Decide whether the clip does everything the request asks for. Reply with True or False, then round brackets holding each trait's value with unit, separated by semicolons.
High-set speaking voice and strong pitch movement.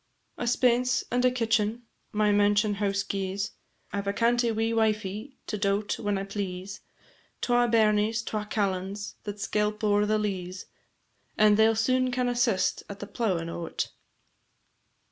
False (210 Hz; 2.4 semitones)